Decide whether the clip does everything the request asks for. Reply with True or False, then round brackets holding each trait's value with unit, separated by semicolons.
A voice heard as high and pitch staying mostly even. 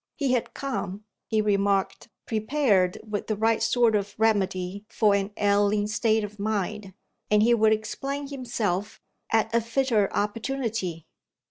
True (215 Hz; 2.3 semitones)